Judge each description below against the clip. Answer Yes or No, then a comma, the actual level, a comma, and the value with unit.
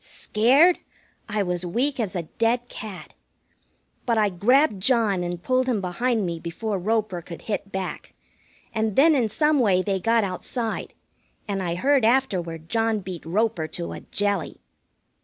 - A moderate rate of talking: Yes, average, 160 wpm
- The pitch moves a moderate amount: Yes, average, 4.6 semitones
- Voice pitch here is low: No, high, 210 Hz